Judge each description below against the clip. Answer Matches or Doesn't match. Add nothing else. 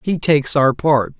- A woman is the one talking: Doesn't match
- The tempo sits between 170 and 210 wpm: Matches